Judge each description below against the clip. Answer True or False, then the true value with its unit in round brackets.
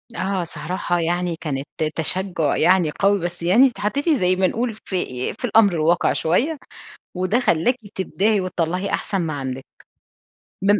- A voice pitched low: False (180 Hz)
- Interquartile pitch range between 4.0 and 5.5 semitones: False (3.5 semitones)